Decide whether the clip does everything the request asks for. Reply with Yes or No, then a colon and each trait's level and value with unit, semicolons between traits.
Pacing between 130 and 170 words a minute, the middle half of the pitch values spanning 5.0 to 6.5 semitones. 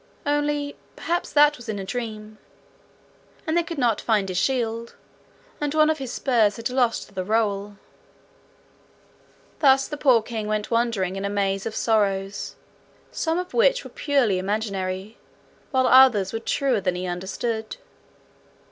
Yes: average, 150 wpm; wide, 5.4 semitones